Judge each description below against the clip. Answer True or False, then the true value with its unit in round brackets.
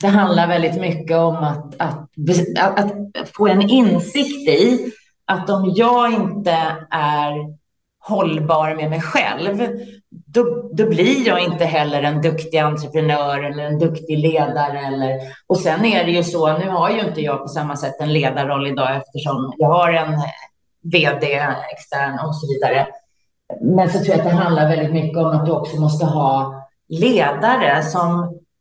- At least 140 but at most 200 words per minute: True (165 wpm)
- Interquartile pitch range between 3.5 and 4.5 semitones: True (4.1 semitones)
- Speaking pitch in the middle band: True (160 Hz)